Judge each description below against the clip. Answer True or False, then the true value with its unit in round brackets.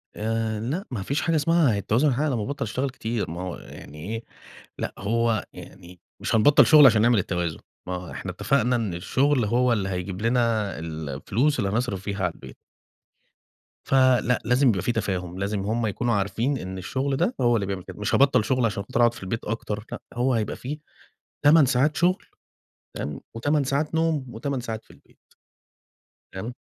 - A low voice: True (115 Hz)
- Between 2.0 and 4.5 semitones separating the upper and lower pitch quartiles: False (5.1 semitones)